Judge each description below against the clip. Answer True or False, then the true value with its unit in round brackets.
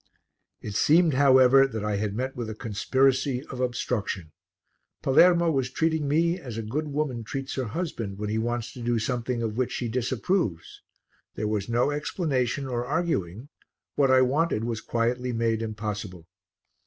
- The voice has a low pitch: True (125 Hz)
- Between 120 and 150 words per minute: False (165 wpm)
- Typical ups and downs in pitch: True (4.0 semitones)